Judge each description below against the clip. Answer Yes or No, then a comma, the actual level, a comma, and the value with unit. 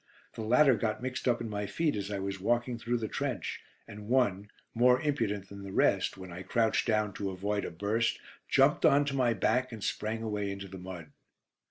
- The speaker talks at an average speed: No, fast, 210 wpm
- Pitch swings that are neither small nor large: Yes, average, 3.3 semitones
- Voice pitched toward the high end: No, low, 110 Hz